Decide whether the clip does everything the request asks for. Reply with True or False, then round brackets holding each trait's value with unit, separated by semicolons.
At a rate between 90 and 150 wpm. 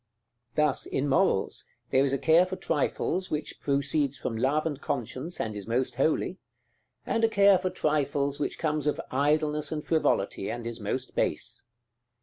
False (165 wpm)